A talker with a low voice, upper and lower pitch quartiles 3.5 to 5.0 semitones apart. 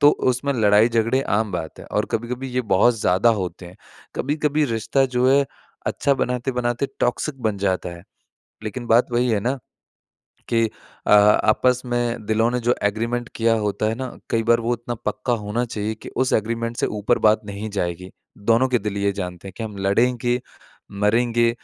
No: low, 115 Hz; average, 2.8 semitones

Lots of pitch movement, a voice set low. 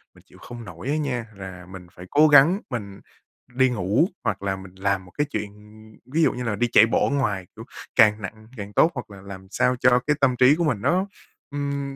Yes: wide, 6.0 semitones; low, 115 Hz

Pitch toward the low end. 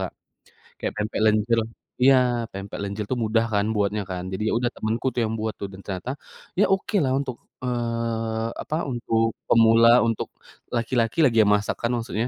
Yes: low, 115 Hz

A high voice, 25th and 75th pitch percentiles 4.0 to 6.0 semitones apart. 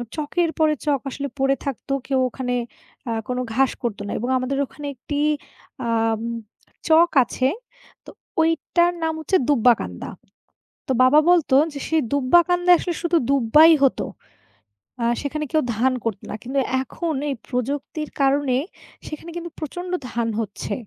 Yes: very high, 280 Hz; average, 4.3 semitones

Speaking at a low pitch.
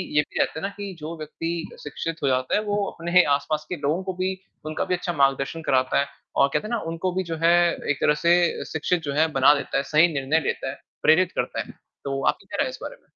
No: medium, 160 Hz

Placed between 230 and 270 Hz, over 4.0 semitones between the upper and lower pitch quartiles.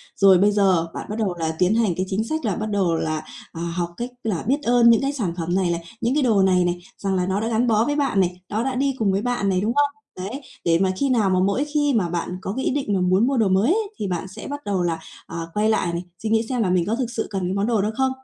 No: high, 205 Hz; average, 4.7 semitones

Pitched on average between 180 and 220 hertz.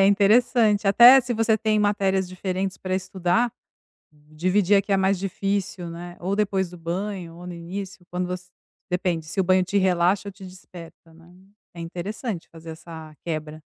Yes: medium, 185 Hz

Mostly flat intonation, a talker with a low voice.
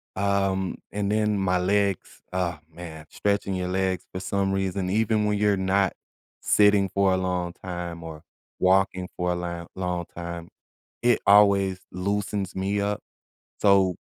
Yes: narrow, 1.9 semitones; very low, 95 Hz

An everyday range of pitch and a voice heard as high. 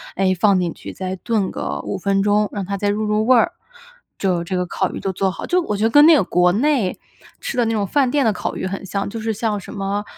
Yes: average, 3.0 semitones; high, 200 Hz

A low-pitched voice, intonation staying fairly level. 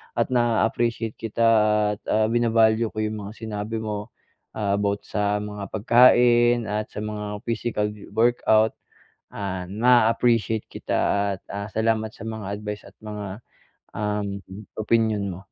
Yes: low, 110 Hz; narrow, 1.6 semitones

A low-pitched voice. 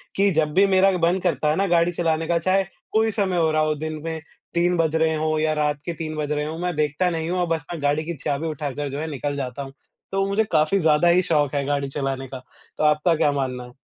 No: medium, 155 Hz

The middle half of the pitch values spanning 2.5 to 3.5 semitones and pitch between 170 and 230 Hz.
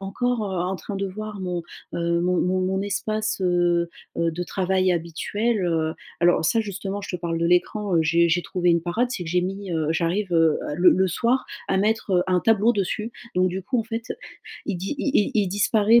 Yes: average, 3.1 semitones; medium, 185 Hz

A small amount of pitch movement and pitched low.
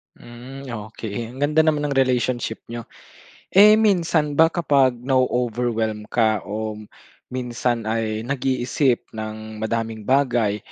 No: average, 3.6 semitones; low, 120 Hz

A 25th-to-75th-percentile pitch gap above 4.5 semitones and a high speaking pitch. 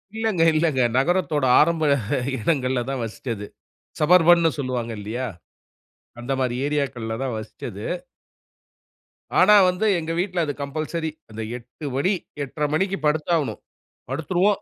No: average, 5.0 semitones; medium, 150 Hz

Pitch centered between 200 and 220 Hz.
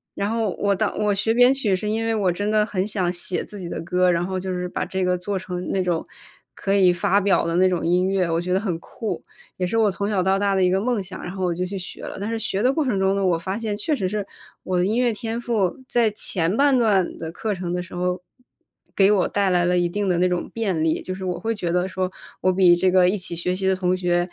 No: high, 190 Hz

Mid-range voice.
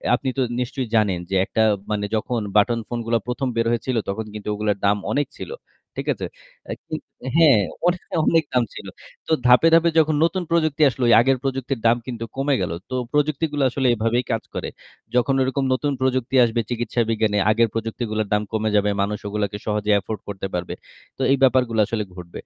No: low, 120 Hz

